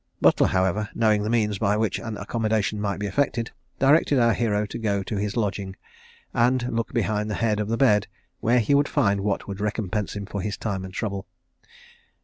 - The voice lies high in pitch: No, low, 105 Hz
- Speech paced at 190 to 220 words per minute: Yes, average, 200 wpm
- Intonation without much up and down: Yes, narrow, 2.3 semitones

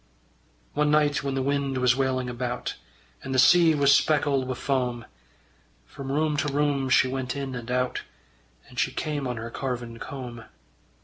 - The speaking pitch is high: No, low, 135 Hz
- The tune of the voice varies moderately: No, narrow, 2.2 semitones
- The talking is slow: No, average, 170 wpm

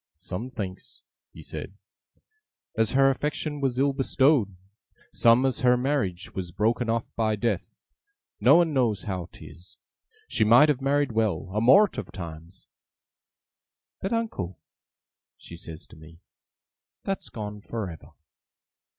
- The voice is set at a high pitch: No, low, 115 Hz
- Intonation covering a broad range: Yes, wide, 6.0 semitones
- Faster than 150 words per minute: No, slow, 135 wpm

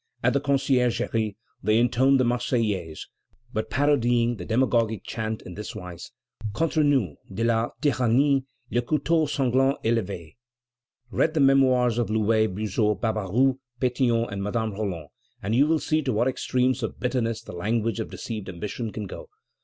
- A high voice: No, low, 115 Hz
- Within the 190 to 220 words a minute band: No, average, 160 wpm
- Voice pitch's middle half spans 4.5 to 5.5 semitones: No, average, 3.4 semitones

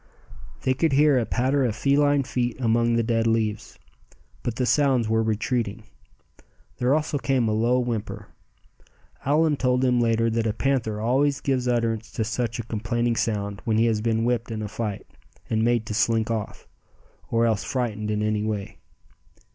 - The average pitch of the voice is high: No, low, 115 Hz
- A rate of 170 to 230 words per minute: Yes, average, 175 wpm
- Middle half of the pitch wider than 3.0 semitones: No, narrow, 2.4 semitones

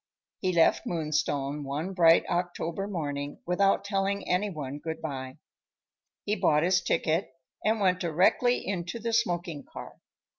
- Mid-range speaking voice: Yes, medium, 175 Hz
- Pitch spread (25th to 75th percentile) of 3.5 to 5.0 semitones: Yes, average, 4.2 semitones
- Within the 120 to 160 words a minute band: Yes, average, 140 wpm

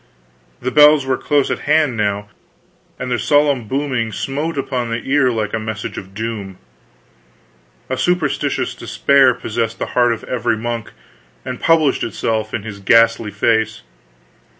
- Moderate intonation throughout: Yes, average, 3.8 semitones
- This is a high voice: No, low, 120 Hz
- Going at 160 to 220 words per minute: No, average, 150 wpm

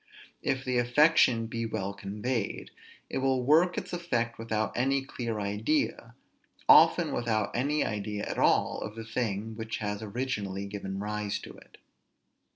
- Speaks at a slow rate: No, average, 150 wpm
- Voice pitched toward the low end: Yes, low, 115 Hz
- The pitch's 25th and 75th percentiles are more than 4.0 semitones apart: No, average, 3.5 semitones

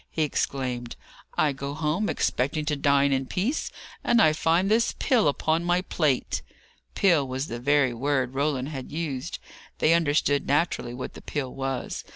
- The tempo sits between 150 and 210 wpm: Yes, average, 165 wpm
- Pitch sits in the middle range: Yes, medium, 145 Hz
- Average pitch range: Yes, average, 3.5 semitones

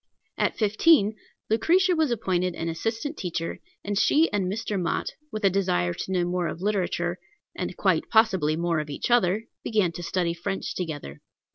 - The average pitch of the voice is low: No, medium, 185 Hz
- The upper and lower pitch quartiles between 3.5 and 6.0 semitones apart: Yes, average, 4.1 semitones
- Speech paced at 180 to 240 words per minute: No, average, 170 wpm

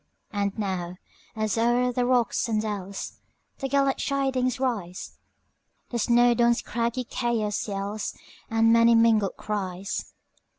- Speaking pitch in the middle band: No, high, 230 Hz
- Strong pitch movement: No, average, 3.1 semitones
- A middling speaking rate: No, slow, 100 wpm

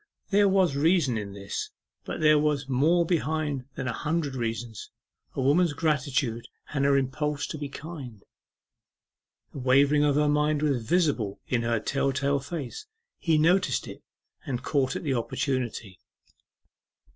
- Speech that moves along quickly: No, average, 150 wpm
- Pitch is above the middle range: No, medium, 140 Hz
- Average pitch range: Yes, average, 3.2 semitones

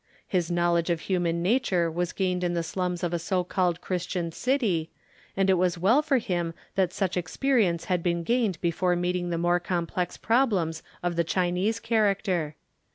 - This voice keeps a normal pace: Yes, average, 175 wpm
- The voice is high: No, medium, 180 Hz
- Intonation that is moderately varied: No, narrow, 2.1 semitones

